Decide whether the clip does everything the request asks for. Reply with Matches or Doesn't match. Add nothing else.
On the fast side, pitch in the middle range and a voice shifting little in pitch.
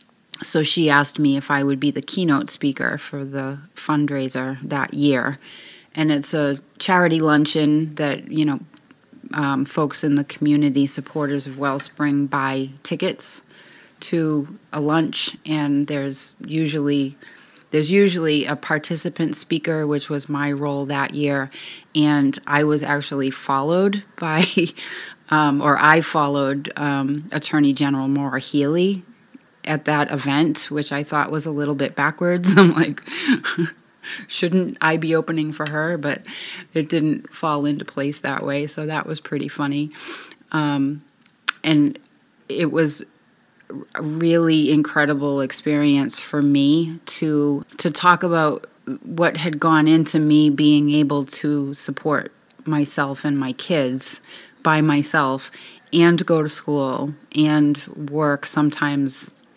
Doesn't match